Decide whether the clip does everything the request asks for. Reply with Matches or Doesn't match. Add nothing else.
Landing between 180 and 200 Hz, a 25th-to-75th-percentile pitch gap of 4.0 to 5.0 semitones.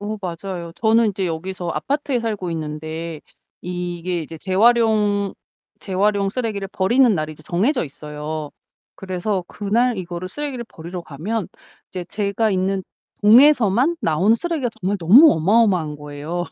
Matches